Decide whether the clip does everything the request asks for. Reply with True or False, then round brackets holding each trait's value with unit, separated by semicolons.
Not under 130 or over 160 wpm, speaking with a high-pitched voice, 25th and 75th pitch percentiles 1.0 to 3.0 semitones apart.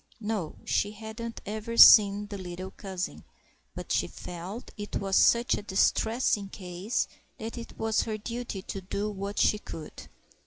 True (155 wpm; 205 Hz; 2.5 semitones)